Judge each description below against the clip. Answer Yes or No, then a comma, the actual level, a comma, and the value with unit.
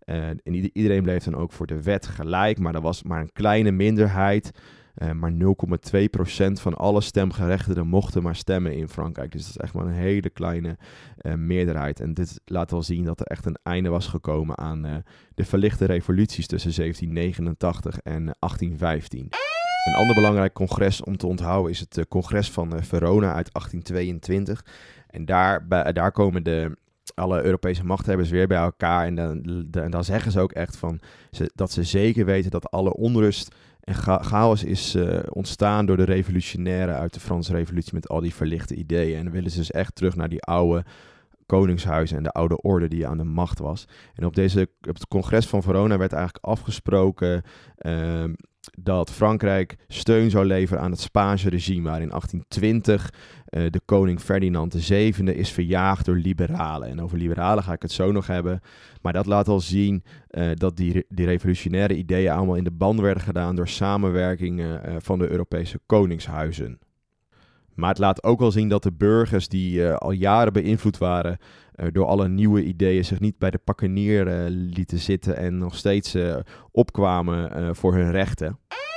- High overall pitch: No, very low, 90 Hz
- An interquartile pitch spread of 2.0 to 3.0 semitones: Yes, narrow, 2.5 semitones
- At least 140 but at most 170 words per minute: No, average, 190 wpm